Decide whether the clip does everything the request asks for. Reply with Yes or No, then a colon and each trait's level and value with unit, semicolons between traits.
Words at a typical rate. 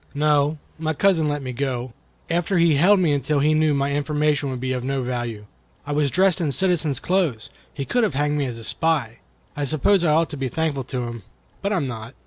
No: fast, 240 wpm